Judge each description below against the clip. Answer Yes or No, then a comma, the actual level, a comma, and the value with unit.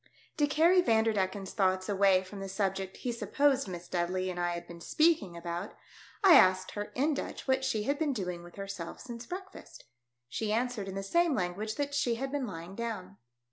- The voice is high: Yes, high, 205 Hz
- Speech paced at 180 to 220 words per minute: Yes, average, 200 wpm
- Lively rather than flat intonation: Yes, wide, 6.0 semitones